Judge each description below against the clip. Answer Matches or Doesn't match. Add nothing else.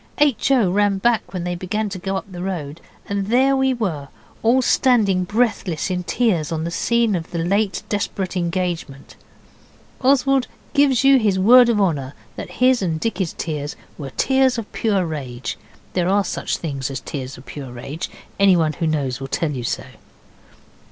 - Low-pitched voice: Doesn't match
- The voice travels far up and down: Matches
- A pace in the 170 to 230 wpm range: Matches